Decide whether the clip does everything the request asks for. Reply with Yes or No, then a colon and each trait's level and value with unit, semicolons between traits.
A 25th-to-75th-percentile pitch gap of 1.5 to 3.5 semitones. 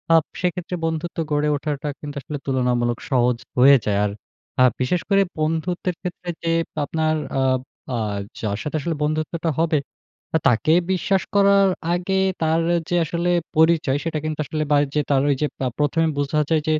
Yes: average, 3.0 semitones